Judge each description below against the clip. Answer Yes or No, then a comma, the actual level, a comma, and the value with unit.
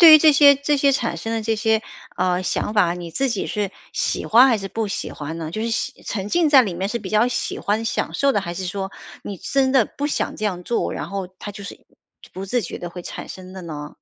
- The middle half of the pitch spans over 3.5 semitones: Yes, average, 5.1 semitones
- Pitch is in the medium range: No, high, 210 Hz